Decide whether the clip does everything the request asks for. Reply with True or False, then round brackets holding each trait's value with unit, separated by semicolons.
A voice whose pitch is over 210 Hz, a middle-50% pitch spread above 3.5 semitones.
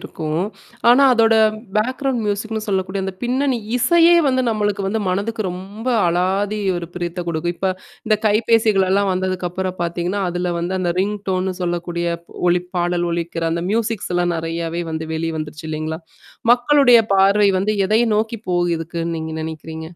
False (185 Hz; 3.9 semitones)